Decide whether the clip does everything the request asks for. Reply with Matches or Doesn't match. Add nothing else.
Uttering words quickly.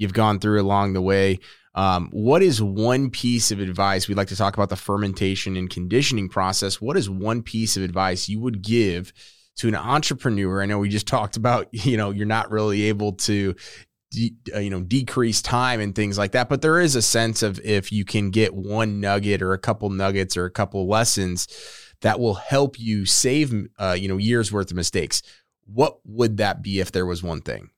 Matches